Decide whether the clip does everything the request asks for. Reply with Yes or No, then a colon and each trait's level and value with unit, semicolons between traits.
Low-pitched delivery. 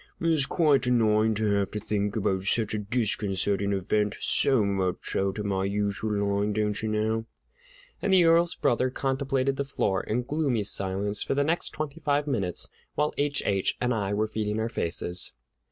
Yes: low, 110 Hz